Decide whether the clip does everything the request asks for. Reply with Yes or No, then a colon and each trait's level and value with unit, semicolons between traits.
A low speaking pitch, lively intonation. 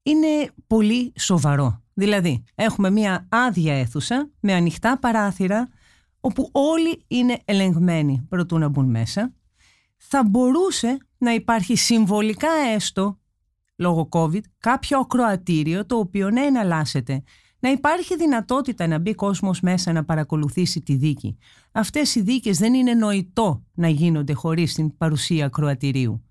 No: high, 200 Hz; wide, 7.2 semitones